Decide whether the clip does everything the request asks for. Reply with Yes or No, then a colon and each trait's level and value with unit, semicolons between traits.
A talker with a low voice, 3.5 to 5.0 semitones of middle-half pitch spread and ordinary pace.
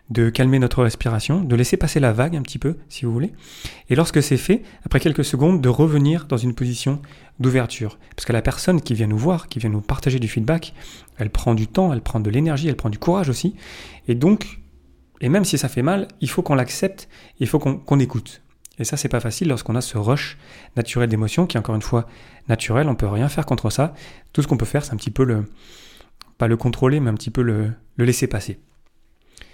No: low, 130 Hz; average, 4.4 semitones; fast, 235 wpm